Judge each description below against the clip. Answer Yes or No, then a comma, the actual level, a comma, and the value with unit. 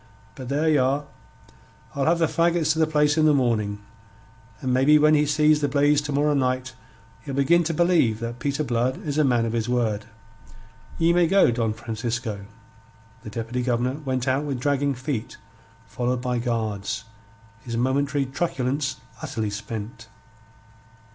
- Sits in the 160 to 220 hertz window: No, low, 130 Hz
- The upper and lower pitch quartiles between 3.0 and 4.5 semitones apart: Yes, average, 3.9 semitones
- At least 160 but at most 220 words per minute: Yes, average, 165 wpm